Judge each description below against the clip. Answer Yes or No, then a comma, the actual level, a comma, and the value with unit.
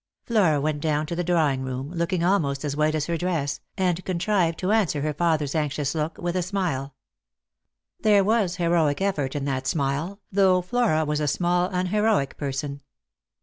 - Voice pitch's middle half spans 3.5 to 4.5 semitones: Yes, average, 4.0 semitones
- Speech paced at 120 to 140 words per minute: No, average, 175 wpm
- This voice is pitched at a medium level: Yes, medium, 165 Hz